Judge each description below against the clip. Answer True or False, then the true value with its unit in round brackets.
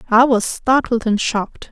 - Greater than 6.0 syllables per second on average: False (4.6 syllables/s)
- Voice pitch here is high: True (230 Hz)